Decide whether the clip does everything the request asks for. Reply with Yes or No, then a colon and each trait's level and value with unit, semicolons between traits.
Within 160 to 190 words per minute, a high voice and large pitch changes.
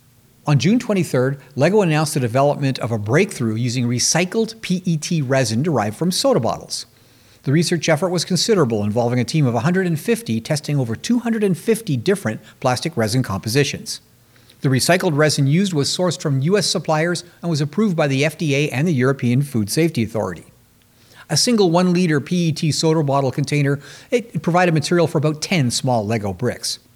No: average, 165 wpm; medium, 150 Hz; wide, 6.1 semitones